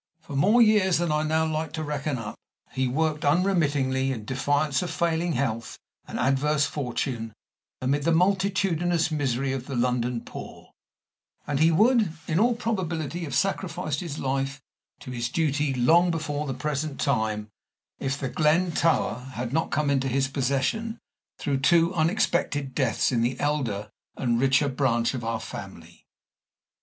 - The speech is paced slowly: No, average, 155 wpm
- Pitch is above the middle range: No, medium, 145 Hz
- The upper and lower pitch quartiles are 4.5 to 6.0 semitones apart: No, average, 3.9 semitones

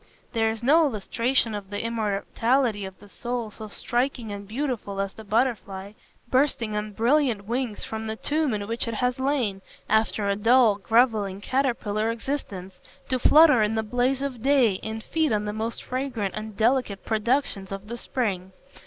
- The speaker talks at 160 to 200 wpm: Yes, average, 170 wpm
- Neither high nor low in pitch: No, high, 225 Hz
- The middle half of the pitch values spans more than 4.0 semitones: No, average, 3.6 semitones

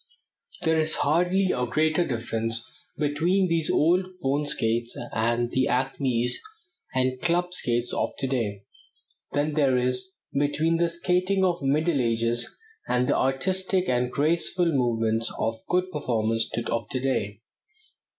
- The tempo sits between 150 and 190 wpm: No, average, 140 wpm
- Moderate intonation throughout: No, wide, 5.9 semitones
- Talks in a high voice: No, low, 135 Hz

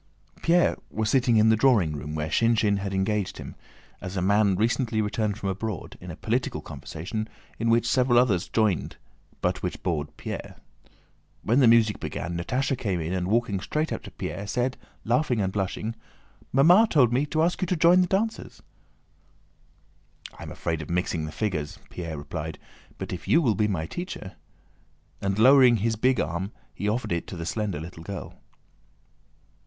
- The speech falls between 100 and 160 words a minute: No, average, 180 wpm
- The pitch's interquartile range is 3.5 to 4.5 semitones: No, average, 5.3 semitones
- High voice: No, low, 105 Hz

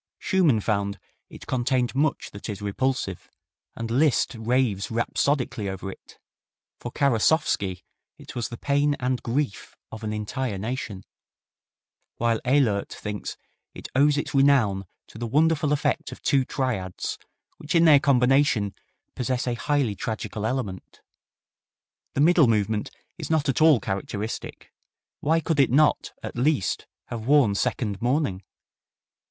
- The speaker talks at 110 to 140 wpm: Yes, slow, 135 wpm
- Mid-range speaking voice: No, low, 125 Hz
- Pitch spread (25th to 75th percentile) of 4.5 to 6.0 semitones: Yes, average, 5.1 semitones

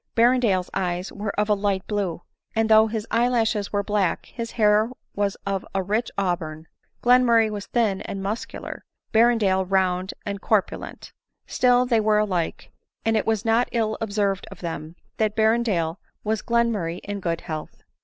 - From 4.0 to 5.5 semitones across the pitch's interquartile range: No, average, 2.9 semitones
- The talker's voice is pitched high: Yes, high, 210 Hz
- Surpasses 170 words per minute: No, average, 165 wpm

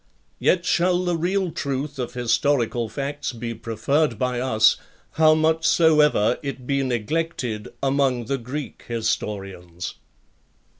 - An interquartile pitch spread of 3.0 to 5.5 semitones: Yes, average, 5.1 semitones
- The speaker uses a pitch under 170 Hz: Yes, low, 135 Hz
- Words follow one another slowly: Yes, slow, 120 wpm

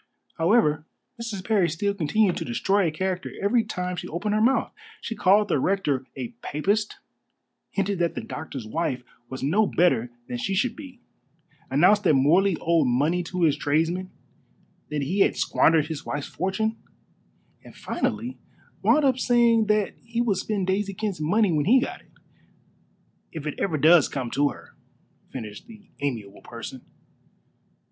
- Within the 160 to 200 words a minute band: Yes, average, 165 wpm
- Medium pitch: Yes, medium, 180 Hz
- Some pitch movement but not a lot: No, wide, 5.8 semitones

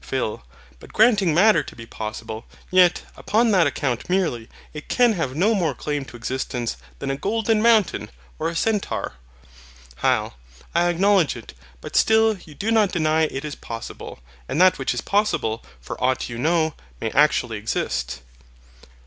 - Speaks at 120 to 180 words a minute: Yes, average, 165 wpm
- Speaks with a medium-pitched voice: Yes, medium, 165 Hz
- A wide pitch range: Yes, wide, 8.1 semitones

